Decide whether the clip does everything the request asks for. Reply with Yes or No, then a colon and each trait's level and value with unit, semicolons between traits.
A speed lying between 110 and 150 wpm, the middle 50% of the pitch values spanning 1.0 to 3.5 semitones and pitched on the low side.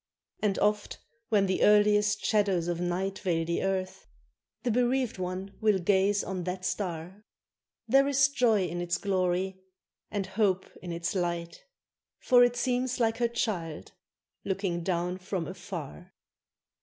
No: average, 145 wpm; average, 3.0 semitones; high, 190 Hz